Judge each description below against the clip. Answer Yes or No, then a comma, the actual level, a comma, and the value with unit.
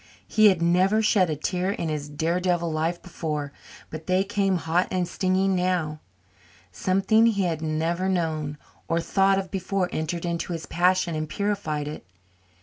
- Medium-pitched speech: Yes, medium, 175 Hz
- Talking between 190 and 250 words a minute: No, average, 160 wpm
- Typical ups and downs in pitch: Yes, average, 3.1 semitones